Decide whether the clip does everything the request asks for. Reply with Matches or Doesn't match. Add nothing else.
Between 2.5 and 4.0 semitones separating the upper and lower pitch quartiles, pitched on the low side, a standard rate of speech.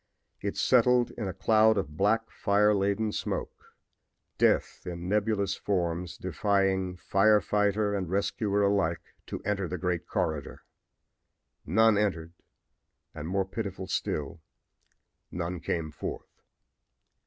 Doesn't match